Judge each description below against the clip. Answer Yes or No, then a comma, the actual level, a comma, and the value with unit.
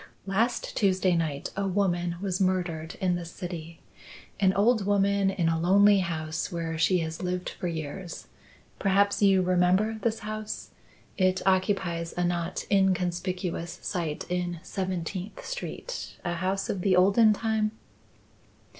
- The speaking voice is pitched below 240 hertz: Yes, medium, 185 Hz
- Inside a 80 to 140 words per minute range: Yes, slow, 135 wpm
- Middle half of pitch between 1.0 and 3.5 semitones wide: Yes, narrow, 2.4 semitones